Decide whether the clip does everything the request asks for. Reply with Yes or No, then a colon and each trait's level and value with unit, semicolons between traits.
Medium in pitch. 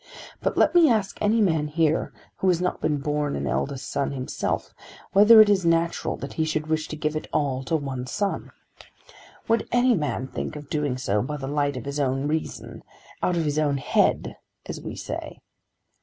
Yes: medium, 150 Hz